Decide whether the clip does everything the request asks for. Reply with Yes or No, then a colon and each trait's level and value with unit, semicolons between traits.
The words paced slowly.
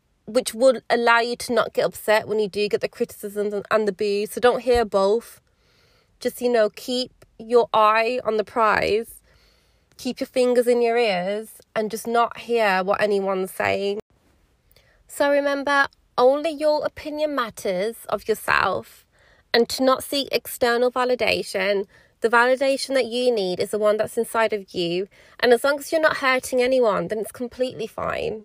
No: average, 170 wpm